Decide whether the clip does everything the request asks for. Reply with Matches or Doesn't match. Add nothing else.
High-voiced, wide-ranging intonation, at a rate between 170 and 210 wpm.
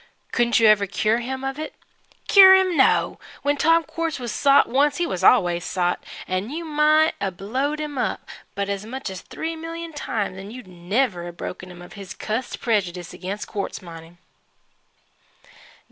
Matches